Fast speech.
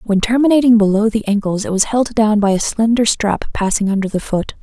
Yes: fast, 220 wpm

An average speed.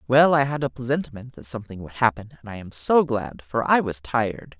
No: fast, 235 wpm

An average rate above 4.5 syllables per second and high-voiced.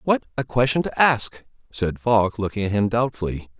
No: 5.0 syllables/s; low, 115 Hz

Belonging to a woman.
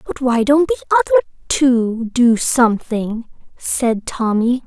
Yes: female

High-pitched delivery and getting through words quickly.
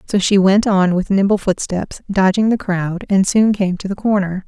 Yes: high, 195 Hz; fast, 215 wpm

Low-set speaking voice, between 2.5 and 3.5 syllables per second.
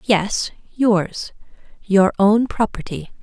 No: high, 205 Hz; 2.9 syllables/s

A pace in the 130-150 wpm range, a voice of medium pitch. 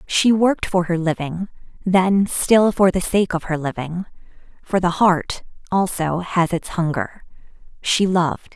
Yes: average, 140 wpm; medium, 180 Hz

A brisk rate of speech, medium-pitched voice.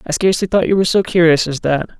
Yes: fast, 270 wpm; medium, 170 Hz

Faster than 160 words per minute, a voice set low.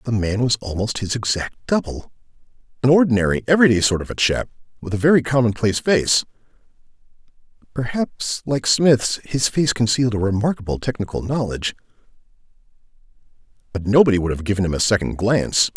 No: average, 145 wpm; low, 115 Hz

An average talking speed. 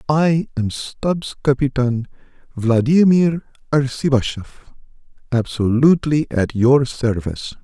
No: slow, 70 wpm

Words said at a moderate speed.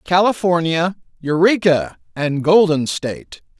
No: slow, 85 wpm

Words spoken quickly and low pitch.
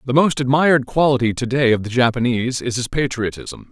No: average, 195 wpm; low, 125 Hz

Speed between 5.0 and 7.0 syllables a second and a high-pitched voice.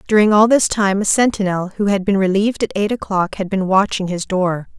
Yes: 5.6 syllables/s; high, 195 Hz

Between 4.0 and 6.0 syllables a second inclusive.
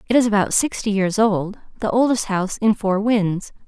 Yes: 5.1 syllables/s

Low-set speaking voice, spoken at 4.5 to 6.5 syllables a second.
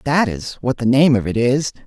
Yes: low, 125 Hz; 5.0 syllables/s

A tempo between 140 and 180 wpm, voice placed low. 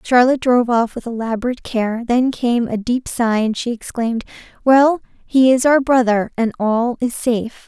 No: average, 170 wpm; high, 240 Hz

